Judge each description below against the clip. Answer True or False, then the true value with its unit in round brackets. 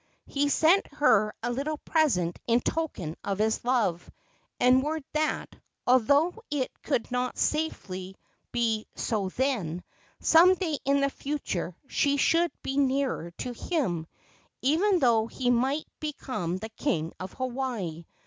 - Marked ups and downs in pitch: True (5.7 semitones)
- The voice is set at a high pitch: True (255 Hz)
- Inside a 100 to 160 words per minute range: True (140 wpm)